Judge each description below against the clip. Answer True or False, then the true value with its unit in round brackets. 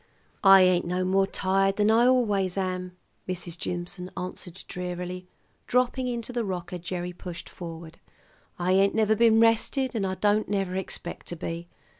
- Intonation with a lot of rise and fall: False (2.9 semitones)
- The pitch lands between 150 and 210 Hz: True (185 Hz)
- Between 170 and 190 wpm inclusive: False (160 wpm)